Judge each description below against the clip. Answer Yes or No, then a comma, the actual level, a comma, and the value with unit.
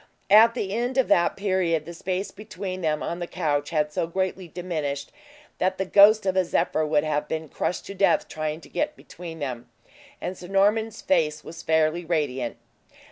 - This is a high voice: No, medium, 175 Hz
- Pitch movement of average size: Yes, average, 4.0 semitones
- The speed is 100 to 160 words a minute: No, average, 190 wpm